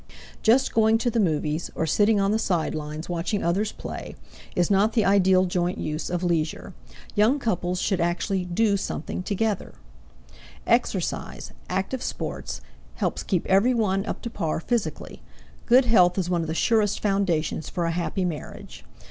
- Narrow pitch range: No, average, 3.9 semitones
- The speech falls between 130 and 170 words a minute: Yes, average, 160 wpm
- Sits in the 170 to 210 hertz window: Yes, high, 190 Hz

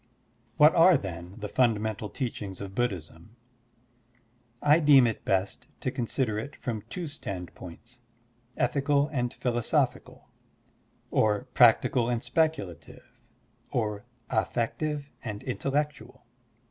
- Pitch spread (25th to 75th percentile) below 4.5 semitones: No, average, 5.3 semitones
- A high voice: No, low, 120 Hz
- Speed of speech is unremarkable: No, slow, 110 wpm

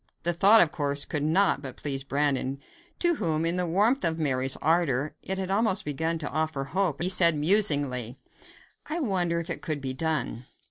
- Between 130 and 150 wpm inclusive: No, average, 195 wpm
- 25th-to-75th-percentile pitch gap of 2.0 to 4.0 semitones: No, average, 4.5 semitones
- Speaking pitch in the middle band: Yes, medium, 160 Hz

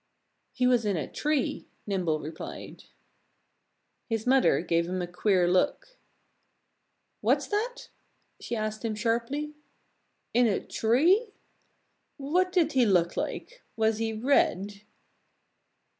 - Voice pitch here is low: No, high, 225 Hz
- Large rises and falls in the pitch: Yes, wide, 6.8 semitones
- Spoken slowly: Yes, slow, 115 wpm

